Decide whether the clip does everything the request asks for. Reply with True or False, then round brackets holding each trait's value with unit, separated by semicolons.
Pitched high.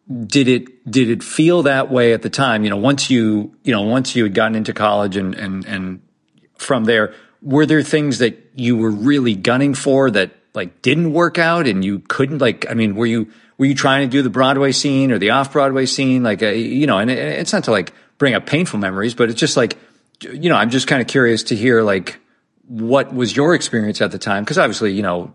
False (125 Hz)